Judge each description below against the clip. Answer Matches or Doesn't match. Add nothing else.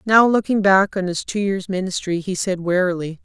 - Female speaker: Matches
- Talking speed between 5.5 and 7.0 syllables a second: Doesn't match